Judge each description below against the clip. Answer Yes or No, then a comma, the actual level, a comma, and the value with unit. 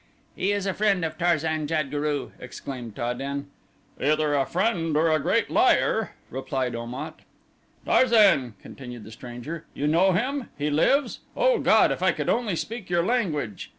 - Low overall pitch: No, medium, 155 Hz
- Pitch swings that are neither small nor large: No, wide, 6.0 semitones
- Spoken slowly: No, average, 170 wpm